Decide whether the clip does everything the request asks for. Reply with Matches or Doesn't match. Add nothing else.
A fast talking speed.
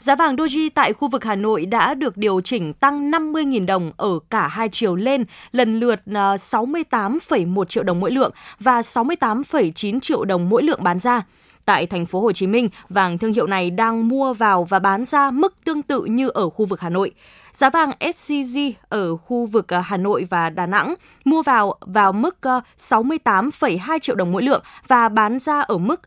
Doesn't match